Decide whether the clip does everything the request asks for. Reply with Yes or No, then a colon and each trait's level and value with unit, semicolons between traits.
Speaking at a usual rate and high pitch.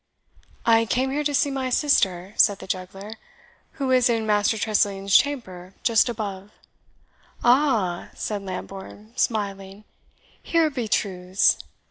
No: slow, 125 wpm; high, 215 Hz